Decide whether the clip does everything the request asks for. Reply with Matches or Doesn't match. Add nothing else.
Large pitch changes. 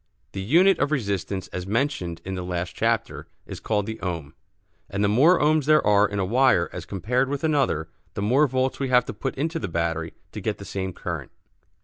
Matches